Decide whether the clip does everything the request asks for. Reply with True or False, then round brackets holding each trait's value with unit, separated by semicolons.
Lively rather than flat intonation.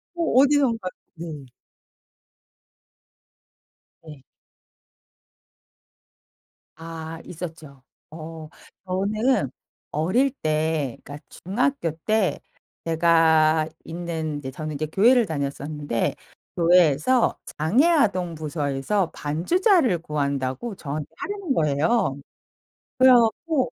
True (6.7 semitones)